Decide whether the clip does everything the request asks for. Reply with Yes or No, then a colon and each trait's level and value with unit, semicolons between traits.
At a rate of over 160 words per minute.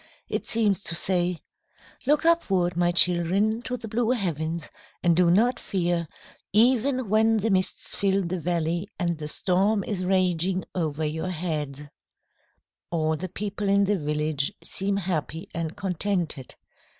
No: average, 145 wpm